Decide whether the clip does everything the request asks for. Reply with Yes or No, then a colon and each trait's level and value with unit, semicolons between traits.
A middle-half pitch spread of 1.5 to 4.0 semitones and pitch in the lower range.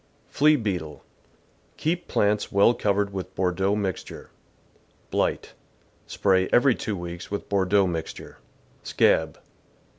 Yes: narrow, 2.4 semitones; low, 100 Hz